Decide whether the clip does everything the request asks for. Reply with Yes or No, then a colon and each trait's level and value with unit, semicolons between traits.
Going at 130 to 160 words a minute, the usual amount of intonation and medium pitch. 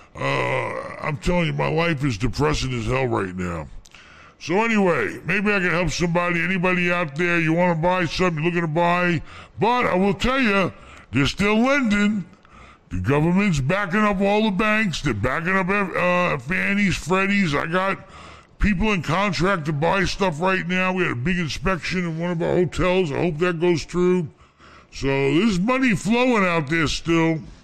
No: average, 180 wpm; average, 4.0 semitones; medium, 175 Hz